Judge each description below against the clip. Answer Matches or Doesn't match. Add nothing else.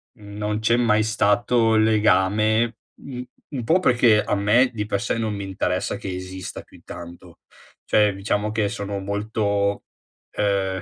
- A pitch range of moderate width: Doesn't match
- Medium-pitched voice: Doesn't match